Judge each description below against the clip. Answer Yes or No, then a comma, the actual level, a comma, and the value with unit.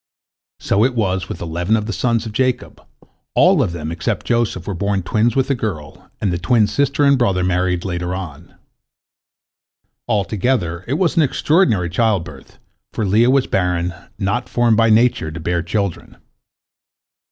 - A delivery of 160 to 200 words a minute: Yes, average, 165 wpm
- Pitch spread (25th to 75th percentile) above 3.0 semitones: Yes, average, 5.2 semitones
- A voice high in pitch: No, low, 100 Hz